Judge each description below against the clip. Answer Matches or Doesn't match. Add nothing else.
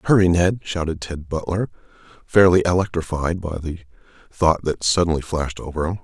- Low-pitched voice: Matches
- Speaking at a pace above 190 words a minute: Doesn't match